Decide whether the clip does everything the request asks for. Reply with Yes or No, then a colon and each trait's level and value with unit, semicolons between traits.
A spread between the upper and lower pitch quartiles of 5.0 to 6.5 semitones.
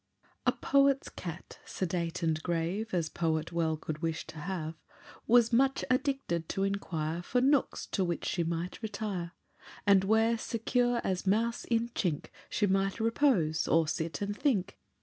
Yes: wide, 5.6 semitones